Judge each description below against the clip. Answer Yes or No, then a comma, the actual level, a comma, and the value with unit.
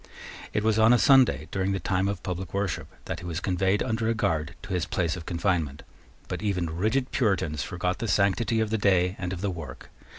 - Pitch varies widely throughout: No, average, 3.4 semitones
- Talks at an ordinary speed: No, fast, 220 wpm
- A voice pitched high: No, very low, 95 Hz